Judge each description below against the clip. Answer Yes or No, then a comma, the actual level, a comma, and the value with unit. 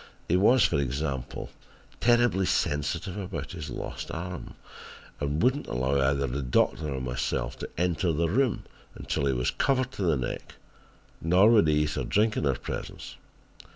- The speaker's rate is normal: Yes, average, 175 wpm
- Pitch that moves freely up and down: Yes, wide, 5.9 semitones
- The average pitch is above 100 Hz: No, very low, 80 Hz